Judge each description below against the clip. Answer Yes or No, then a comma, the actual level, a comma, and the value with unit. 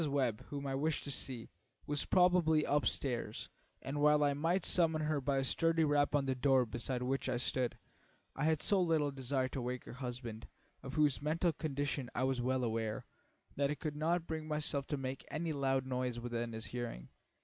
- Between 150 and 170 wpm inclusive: No, average, 200 wpm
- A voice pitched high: No, medium, 140 Hz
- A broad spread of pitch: No, average, 3.1 semitones